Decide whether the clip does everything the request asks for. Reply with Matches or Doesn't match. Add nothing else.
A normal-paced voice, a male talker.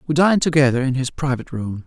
Doesn't match